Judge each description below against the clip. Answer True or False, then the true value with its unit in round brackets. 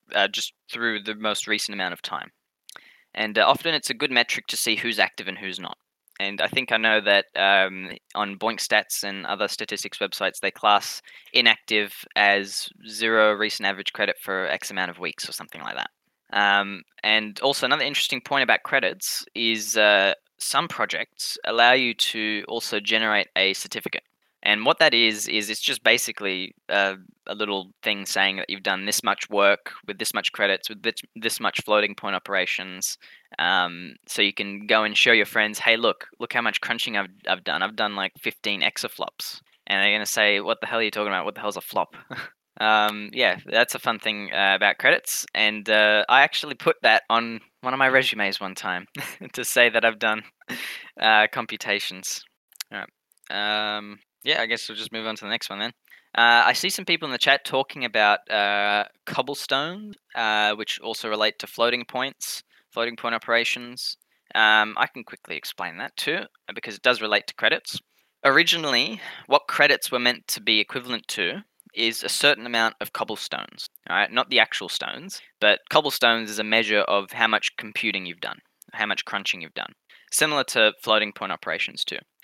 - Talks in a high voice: False (110 Hz)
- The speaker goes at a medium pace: True (195 wpm)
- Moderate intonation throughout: False (2.1 semitones)